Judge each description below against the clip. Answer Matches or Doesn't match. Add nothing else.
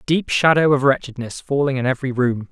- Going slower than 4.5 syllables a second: Doesn't match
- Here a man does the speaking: Matches